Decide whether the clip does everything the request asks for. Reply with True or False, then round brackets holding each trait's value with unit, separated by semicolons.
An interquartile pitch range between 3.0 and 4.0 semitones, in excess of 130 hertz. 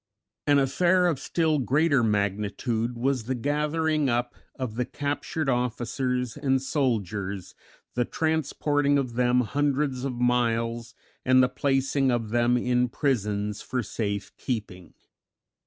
False (3.4 semitones; 125 Hz)